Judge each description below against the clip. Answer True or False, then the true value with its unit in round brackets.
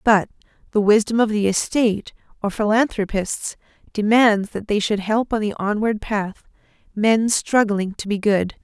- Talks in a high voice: True (210 Hz)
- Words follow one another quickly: False (155 wpm)